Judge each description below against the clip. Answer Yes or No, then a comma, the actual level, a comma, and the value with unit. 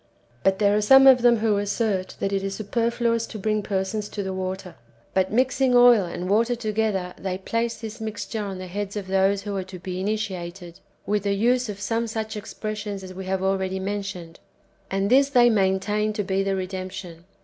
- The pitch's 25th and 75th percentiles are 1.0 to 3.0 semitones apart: Yes, narrow, 2.5 semitones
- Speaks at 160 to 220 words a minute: Yes, fast, 205 wpm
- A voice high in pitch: Yes, high, 200 Hz